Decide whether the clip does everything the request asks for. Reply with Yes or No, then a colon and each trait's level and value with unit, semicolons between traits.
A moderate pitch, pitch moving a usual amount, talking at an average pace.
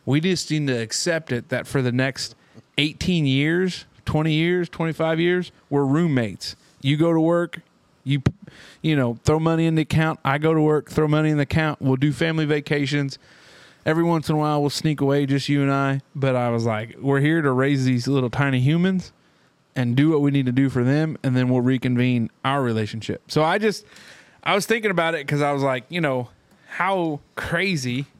No: medium, 145 Hz; average, 3.5 semitones; fast, 210 wpm